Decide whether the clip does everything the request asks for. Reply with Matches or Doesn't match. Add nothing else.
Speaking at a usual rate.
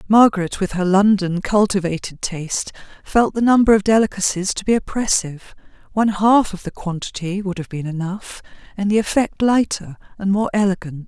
Matches